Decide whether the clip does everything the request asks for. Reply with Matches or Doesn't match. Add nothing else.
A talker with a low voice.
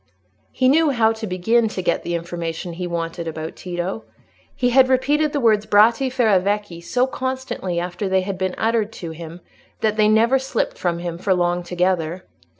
Doesn't match